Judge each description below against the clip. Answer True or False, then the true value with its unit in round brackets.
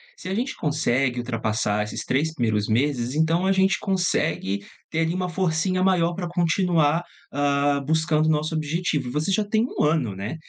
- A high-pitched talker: False (155 Hz)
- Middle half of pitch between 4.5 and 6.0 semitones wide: True (5.3 semitones)